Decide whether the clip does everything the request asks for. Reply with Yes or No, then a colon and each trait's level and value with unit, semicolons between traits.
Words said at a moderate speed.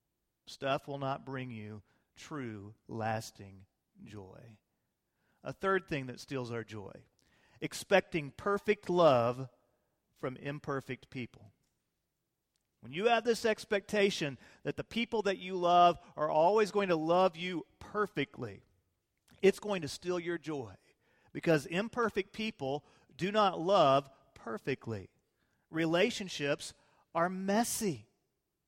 No: slow, 115 wpm